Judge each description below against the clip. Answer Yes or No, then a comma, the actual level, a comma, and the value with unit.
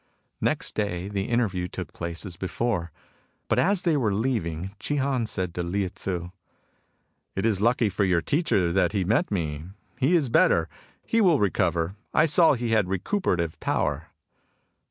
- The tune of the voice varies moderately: No, wide, 5.7 semitones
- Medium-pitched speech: No, low, 100 Hz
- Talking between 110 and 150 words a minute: No, average, 170 wpm